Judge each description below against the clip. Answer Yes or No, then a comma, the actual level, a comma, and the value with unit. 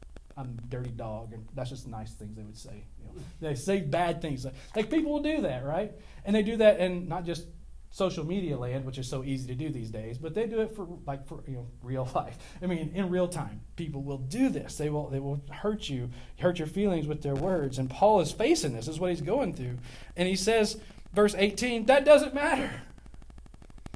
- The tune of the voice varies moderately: No, wide, 6.9 semitones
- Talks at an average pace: No, fast, 235 wpm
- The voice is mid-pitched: Yes, medium, 160 Hz